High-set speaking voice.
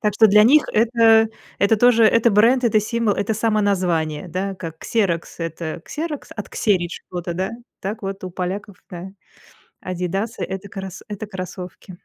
Yes: high, 200 Hz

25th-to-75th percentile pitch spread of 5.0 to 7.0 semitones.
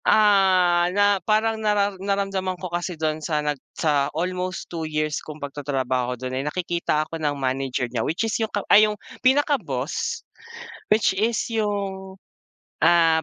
Yes: average, 5.3 semitones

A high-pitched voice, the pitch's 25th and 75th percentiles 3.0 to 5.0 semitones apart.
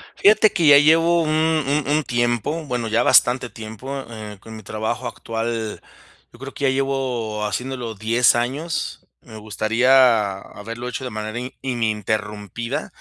No: low, 120 Hz; average, 3.8 semitones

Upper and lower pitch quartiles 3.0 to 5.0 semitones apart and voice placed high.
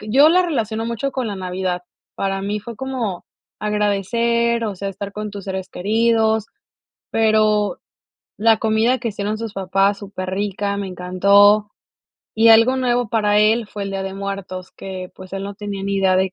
No: narrow, 2.6 semitones; high, 205 Hz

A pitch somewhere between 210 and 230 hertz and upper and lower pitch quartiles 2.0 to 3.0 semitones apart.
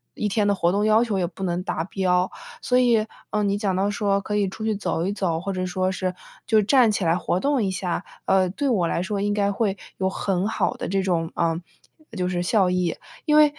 No: high, 195 Hz; narrow, 2.6 semitones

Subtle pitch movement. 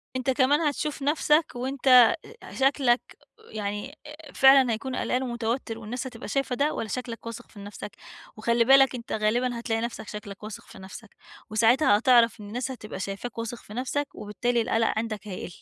No: average, 3.5 semitones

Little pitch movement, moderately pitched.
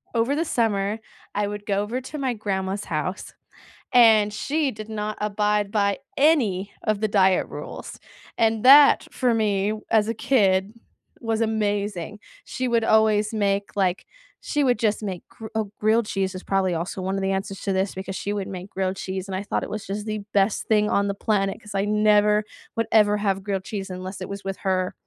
No: narrow, 2.1 semitones; high, 205 Hz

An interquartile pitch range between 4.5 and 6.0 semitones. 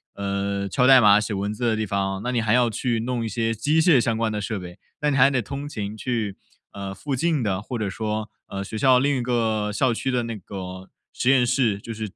No: average, 3.7 semitones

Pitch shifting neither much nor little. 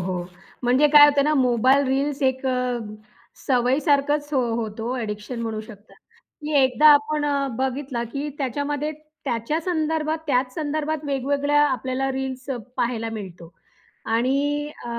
Yes: average, 3.1 semitones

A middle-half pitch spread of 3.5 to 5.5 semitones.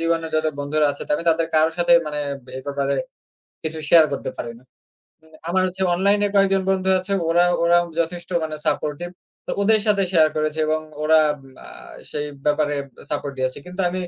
No: average, 3.1 semitones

